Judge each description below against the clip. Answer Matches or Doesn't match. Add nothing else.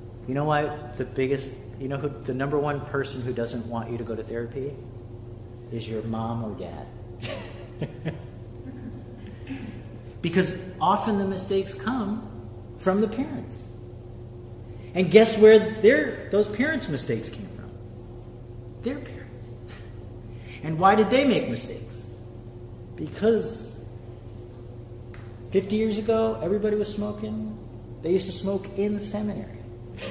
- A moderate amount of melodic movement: Doesn't match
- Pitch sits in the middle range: Doesn't match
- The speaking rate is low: Matches